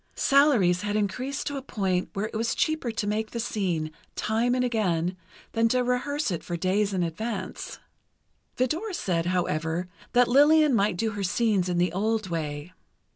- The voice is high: Yes, high, 210 Hz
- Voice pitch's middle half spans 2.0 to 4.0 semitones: No, wide, 5.4 semitones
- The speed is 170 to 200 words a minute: Yes, average, 175 wpm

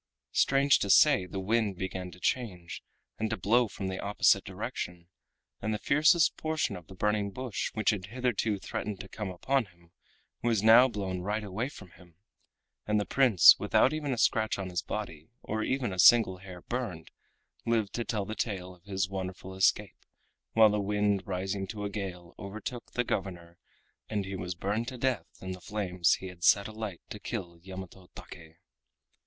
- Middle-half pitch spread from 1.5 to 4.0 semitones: Yes, average, 3.3 semitones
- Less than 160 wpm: No, average, 180 wpm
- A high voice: No, low, 100 Hz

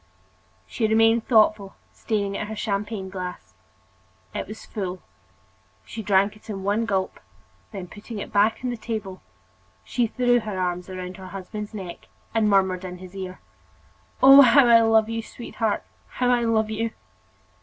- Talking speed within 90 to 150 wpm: No, average, 160 wpm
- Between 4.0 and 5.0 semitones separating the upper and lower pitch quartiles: No, average, 3.0 semitones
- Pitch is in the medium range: No, high, 210 Hz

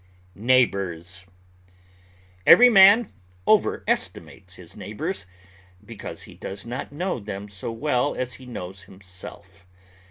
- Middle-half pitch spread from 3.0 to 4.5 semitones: No, average, 5.1 semitones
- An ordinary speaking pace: No, slow, 105 wpm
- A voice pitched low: Yes, low, 115 Hz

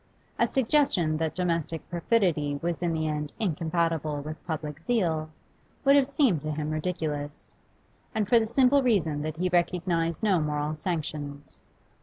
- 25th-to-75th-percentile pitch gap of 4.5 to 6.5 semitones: No, average, 3.5 semitones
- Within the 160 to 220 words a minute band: No, average, 150 wpm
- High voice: No, medium, 165 Hz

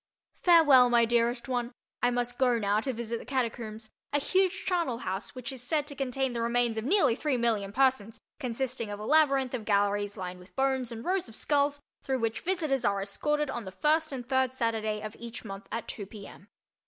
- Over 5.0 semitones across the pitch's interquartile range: No, average, 3.6 semitones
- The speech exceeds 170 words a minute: Yes, fast, 205 wpm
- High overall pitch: Yes, high, 245 Hz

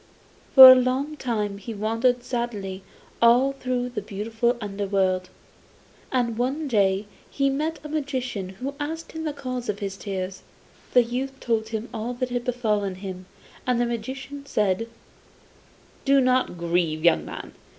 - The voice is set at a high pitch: Yes, high, 235 Hz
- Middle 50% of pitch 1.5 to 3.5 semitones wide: No, average, 4.4 semitones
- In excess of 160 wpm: No, average, 150 wpm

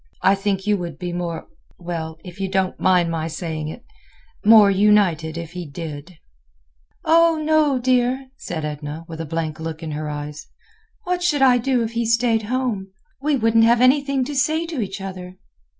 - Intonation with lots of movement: Yes, wide, 7.5 semitones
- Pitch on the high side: Yes, high, 195 Hz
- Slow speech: No, average, 175 wpm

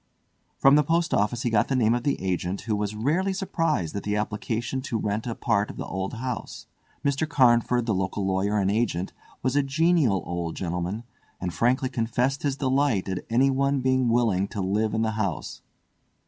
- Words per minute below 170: No, average, 190 wpm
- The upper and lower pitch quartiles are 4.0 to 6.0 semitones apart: Yes, average, 4.8 semitones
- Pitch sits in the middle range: No, low, 115 Hz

